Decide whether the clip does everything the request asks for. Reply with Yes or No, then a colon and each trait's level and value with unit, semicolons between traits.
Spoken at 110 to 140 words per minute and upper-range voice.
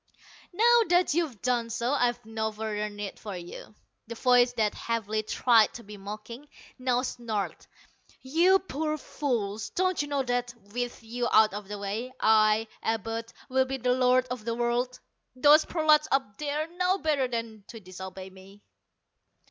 No: average, 165 wpm; high, 240 Hz